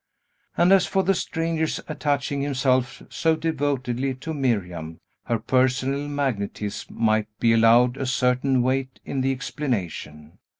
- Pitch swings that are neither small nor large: Yes, average, 3.6 semitones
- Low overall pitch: Yes, low, 130 Hz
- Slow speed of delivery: Yes, slow, 130 wpm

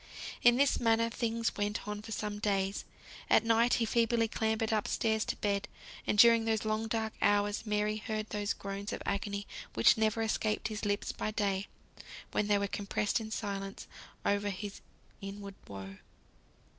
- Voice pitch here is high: Yes, high, 210 Hz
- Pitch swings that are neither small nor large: No, narrow, 1.7 semitones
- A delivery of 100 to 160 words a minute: No, average, 170 wpm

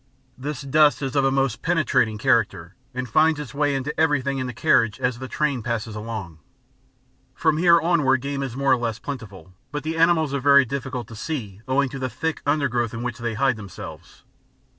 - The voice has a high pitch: No, low, 135 Hz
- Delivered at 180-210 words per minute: Yes, average, 200 wpm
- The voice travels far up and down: No, average, 4.0 semitones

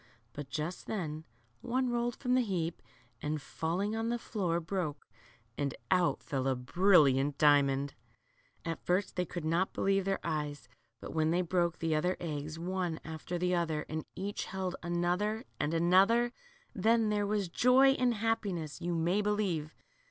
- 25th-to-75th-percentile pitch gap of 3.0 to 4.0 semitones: No, average, 4.5 semitones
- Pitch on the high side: No, medium, 175 Hz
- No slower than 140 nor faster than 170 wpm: Yes, average, 165 wpm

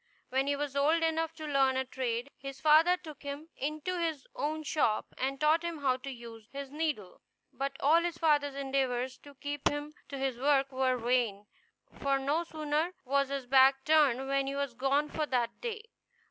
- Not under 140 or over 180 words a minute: No, average, 190 wpm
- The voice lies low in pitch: No, very high, 280 Hz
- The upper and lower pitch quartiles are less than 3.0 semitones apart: Yes, narrow, 2.6 semitones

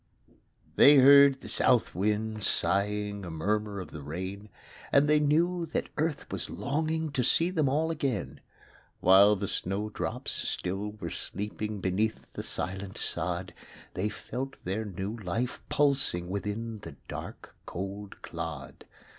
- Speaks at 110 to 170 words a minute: Yes, average, 140 wpm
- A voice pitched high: No, low, 105 Hz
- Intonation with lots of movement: Yes, wide, 6.1 semitones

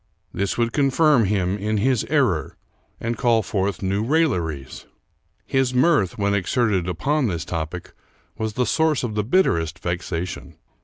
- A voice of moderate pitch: No, low, 105 Hz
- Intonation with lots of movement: Yes, wide, 6.0 semitones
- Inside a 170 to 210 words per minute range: No, average, 150 wpm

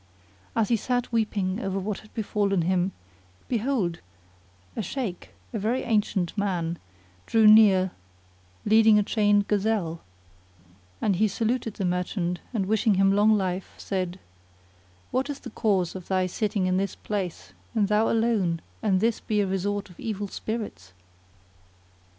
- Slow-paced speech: No, average, 145 wpm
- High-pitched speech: Yes, high, 205 Hz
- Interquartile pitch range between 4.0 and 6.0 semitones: No, average, 2.8 semitones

